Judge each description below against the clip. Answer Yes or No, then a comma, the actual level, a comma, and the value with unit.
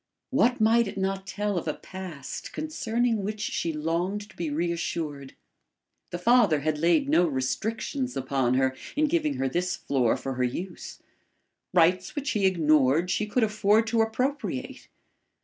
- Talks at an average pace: Yes, average, 155 wpm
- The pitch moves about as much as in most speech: No, wide, 6.3 semitones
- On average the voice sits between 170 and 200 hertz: Yes, high, 190 Hz